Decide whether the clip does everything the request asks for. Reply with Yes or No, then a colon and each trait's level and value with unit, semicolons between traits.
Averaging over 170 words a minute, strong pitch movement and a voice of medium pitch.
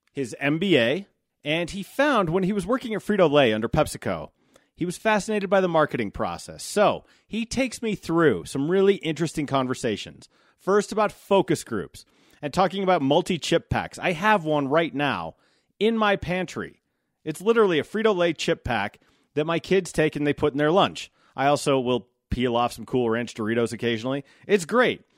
Yes: average, 185 wpm; wide, 6.3 semitones; medium, 160 Hz